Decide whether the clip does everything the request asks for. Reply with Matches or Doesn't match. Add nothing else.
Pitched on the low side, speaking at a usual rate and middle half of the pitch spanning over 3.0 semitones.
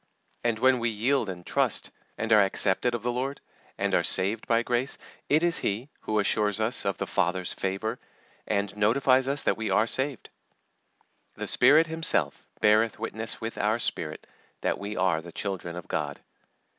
Matches